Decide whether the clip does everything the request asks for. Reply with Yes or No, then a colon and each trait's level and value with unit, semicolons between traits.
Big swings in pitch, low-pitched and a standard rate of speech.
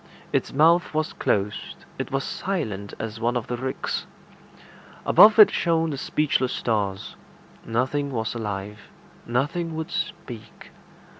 No: wide, 6.3 semitones; low, 130 Hz; slow, 130 wpm